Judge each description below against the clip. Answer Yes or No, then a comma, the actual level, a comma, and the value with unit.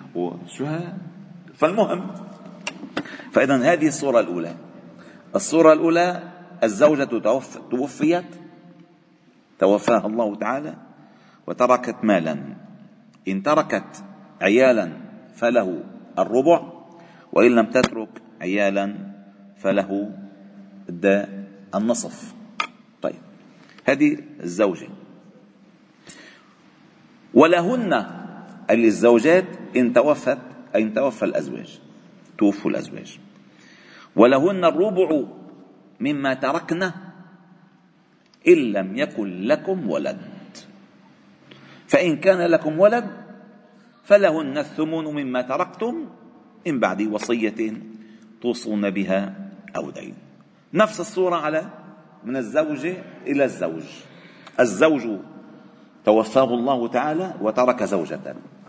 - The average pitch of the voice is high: No, medium, 170 Hz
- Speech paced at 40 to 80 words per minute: Yes, average, 75 wpm